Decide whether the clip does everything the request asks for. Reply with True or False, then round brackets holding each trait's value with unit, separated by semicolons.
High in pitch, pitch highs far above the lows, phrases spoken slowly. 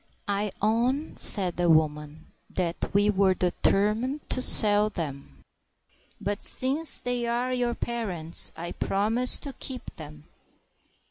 True (205 Hz; 6.1 semitones; 125 wpm)